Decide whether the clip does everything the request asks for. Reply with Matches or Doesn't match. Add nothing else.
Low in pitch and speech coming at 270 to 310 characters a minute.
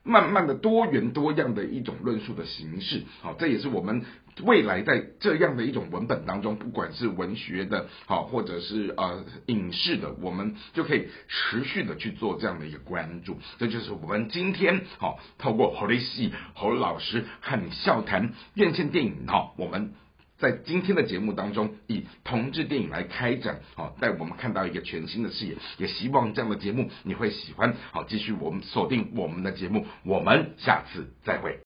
Matches